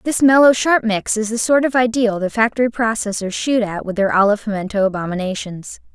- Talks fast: No, average, 190 wpm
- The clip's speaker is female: Yes, female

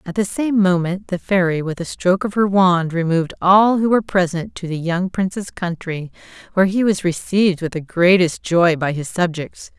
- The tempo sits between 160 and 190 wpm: No, average, 200 wpm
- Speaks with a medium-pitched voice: Yes, medium, 180 Hz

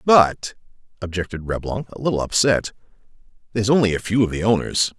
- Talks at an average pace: Yes, average, 155 wpm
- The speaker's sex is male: Yes, male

